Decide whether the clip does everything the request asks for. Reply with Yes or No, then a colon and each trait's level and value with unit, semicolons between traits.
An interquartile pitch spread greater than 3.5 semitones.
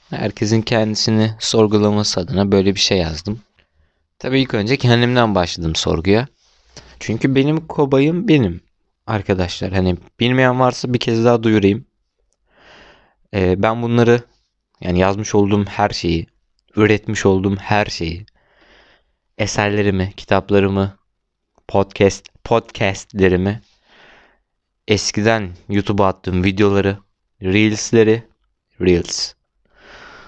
No: average, 3.1 semitones